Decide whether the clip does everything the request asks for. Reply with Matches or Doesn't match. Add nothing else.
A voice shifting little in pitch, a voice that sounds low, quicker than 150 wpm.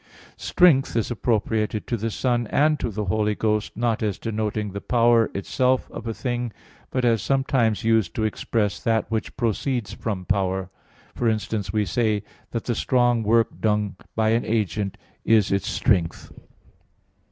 Matches